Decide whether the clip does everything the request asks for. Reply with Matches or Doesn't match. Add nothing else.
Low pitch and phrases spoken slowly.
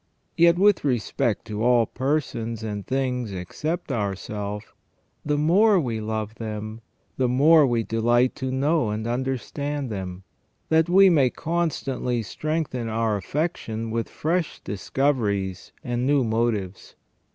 Matches